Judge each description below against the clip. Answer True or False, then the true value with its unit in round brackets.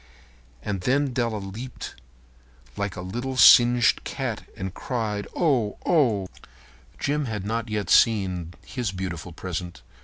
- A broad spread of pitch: False (5.0 semitones)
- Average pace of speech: False (130 wpm)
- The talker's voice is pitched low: True (105 Hz)